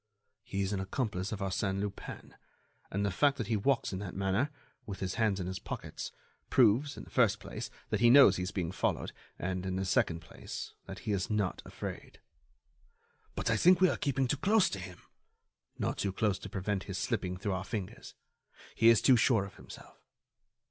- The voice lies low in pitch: Yes, low, 100 Hz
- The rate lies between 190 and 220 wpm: Yes, fast, 205 wpm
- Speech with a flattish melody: No, average, 3.6 semitones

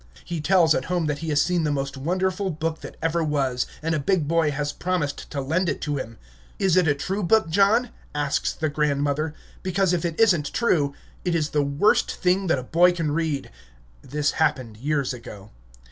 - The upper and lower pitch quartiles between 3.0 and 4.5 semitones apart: Yes, average, 3.8 semitones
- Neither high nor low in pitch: Yes, medium, 155 Hz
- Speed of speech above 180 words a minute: Yes, fast, 205 wpm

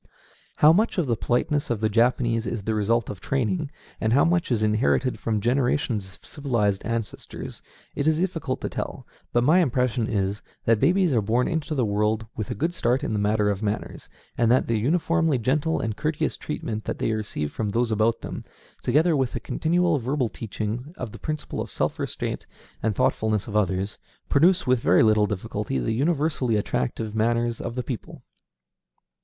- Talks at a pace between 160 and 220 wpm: Yes, average, 185 wpm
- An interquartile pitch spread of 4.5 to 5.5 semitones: Yes, average, 5.2 semitones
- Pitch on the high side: No, low, 120 Hz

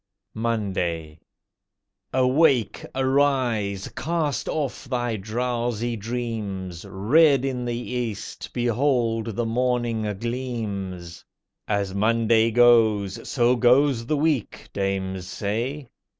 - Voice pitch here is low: Yes, low, 115 Hz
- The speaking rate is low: Yes, slow, 95 wpm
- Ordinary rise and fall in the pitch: Yes, average, 3.8 semitones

